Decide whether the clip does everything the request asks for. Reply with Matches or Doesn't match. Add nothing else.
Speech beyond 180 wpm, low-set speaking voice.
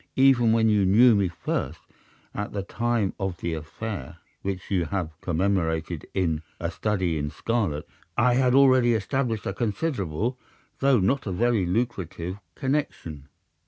Doesn't match